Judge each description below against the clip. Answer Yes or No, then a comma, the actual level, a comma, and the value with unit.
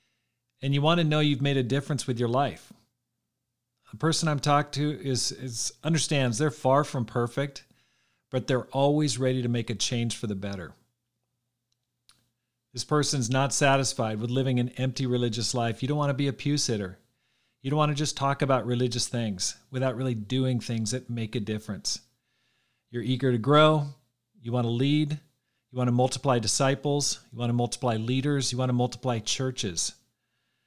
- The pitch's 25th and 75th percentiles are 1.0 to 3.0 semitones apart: Yes, narrow, 2.6 semitones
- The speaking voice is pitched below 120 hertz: No, low, 125 Hz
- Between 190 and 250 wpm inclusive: No, average, 180 wpm